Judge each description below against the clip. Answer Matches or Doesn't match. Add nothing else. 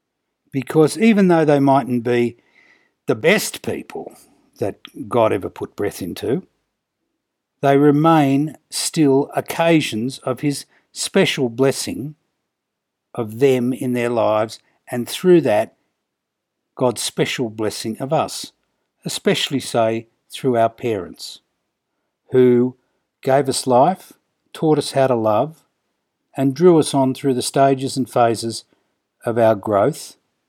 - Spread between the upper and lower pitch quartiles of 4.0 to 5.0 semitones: Doesn't match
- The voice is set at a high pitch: Doesn't match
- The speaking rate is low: Matches